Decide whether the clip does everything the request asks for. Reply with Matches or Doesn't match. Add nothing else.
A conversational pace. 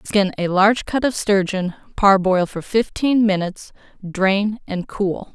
Matches